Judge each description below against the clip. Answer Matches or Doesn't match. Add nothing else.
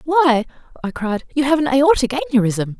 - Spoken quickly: Doesn't match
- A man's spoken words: Doesn't match